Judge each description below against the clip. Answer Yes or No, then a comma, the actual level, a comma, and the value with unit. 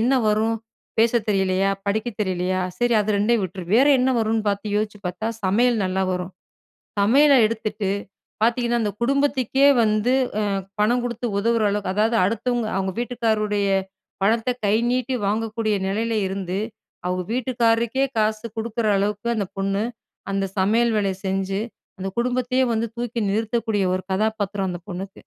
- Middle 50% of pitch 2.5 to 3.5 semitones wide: Yes, average, 3.1 semitones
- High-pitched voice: Yes, high, 215 Hz